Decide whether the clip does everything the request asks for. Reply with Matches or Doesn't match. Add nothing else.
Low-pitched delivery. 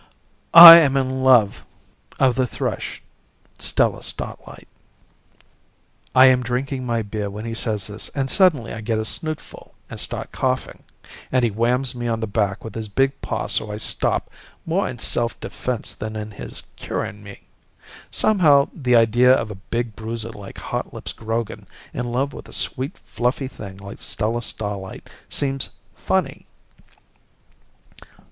Matches